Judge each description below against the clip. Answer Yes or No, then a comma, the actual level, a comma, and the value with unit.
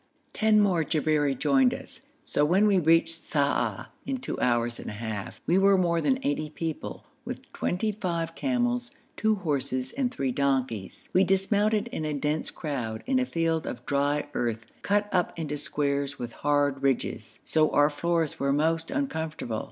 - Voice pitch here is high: No, medium, 155 Hz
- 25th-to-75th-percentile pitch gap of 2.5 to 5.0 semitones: No, wide, 5.5 semitones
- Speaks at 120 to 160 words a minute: No, average, 170 wpm